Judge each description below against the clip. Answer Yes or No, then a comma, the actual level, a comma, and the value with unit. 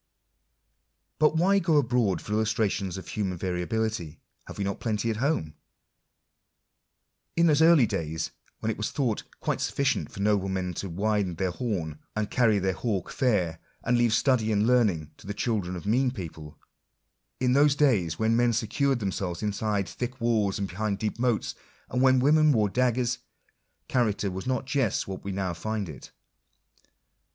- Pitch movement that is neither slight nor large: Yes, average, 4.7 semitones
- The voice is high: No, low, 110 Hz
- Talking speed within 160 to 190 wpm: Yes, average, 165 wpm